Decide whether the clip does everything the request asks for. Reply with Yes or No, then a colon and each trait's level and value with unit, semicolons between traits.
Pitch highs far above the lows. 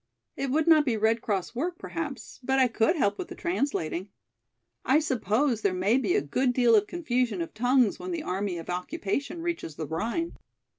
Yes: wide, 6.5 semitones